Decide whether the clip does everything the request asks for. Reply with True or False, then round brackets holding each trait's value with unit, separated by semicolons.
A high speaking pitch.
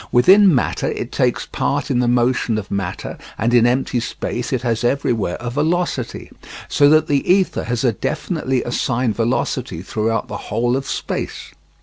False (120 Hz)